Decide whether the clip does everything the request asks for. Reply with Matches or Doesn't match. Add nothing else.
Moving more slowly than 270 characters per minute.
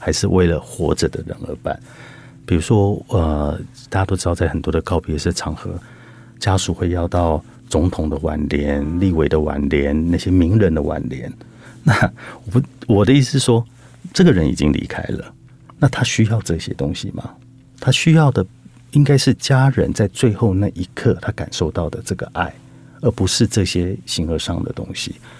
Matches